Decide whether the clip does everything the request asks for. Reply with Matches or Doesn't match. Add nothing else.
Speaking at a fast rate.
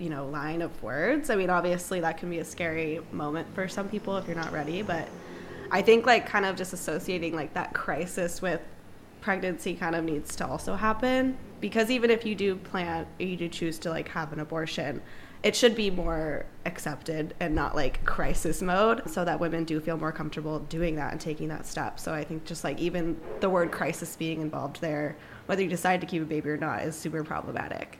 Matches